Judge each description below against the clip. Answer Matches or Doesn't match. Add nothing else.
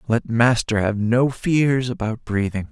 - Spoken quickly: Doesn't match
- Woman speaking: Doesn't match